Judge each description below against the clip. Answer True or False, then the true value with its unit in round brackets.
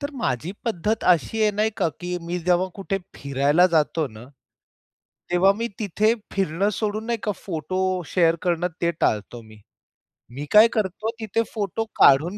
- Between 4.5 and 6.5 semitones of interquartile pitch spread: True (5.1 semitones)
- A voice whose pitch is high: False (180 Hz)